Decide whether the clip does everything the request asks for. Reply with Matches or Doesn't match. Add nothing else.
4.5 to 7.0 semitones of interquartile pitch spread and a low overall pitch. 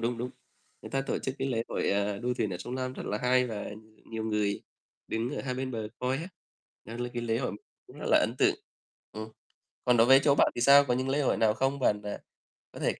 Doesn't match